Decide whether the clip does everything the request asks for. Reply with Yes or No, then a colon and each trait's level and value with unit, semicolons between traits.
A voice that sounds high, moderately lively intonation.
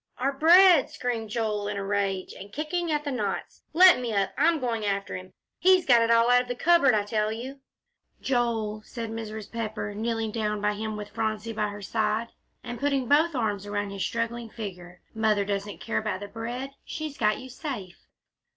Yes: high, 225 Hz; average, 3.6 semitones